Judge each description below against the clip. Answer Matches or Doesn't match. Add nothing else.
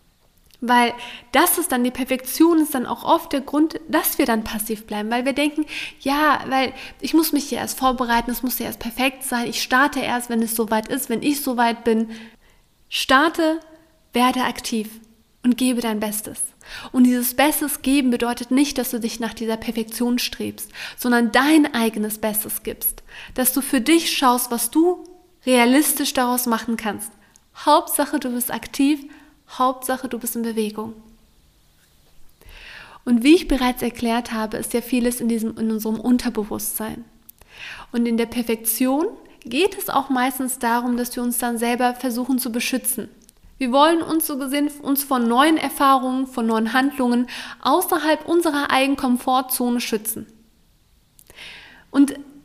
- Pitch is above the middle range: Matches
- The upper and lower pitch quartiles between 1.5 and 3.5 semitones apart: Matches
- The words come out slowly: Doesn't match